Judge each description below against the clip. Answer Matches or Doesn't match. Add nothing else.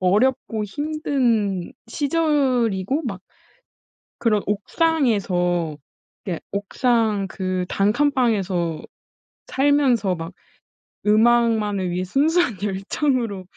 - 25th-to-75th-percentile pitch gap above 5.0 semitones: Matches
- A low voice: Doesn't match